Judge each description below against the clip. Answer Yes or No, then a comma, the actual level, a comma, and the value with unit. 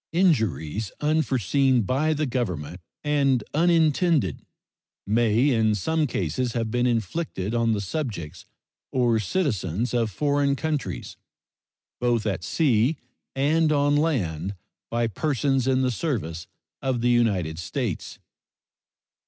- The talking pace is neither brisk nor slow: No, slow, 115 wpm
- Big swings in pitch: Yes, wide, 5.7 semitones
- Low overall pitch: Yes, low, 120 Hz